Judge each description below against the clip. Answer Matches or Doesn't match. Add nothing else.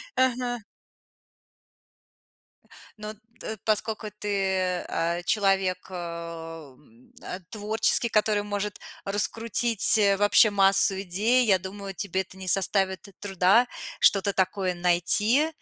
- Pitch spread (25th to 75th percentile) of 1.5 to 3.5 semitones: Matches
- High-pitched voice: Matches